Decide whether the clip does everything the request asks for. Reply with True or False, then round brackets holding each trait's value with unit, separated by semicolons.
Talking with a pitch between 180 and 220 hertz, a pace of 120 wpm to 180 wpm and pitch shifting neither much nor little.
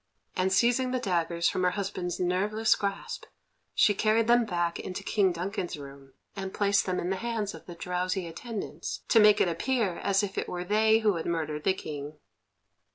False (190 Hz; 190 wpm; 3.5 semitones)